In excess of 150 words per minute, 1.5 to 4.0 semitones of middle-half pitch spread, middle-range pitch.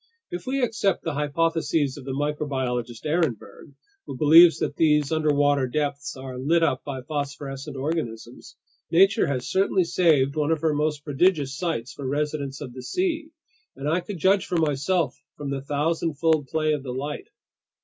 Yes: average, 160 wpm; average, 3.1 semitones; medium, 150 Hz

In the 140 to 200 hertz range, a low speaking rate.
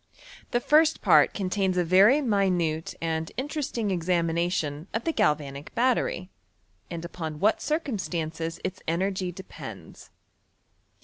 Yes: medium, 185 Hz; slow, 120 wpm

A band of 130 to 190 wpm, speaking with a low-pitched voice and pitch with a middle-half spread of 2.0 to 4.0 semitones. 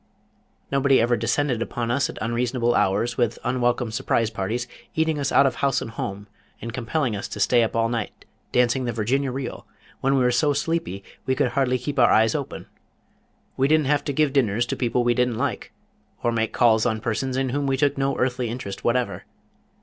No: fast, 205 wpm; low, 125 Hz; average, 2.8 semitones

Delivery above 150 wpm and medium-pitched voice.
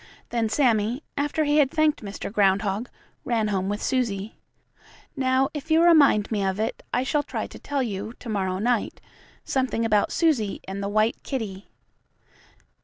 No: average, 165 wpm; high, 225 Hz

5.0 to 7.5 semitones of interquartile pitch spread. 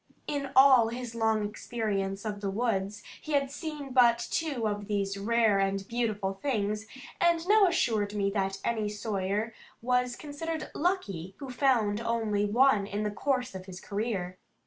No: average, 4.3 semitones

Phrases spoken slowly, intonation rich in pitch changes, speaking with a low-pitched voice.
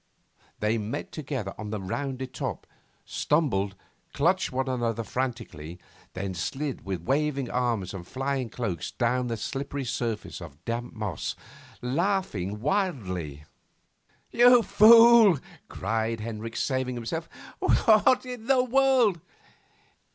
Yes: slow, 115 wpm; wide, 7.5 semitones; low, 125 Hz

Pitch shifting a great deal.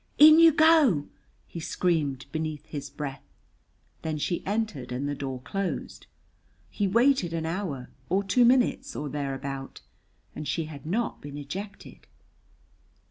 Yes: wide, 6.6 semitones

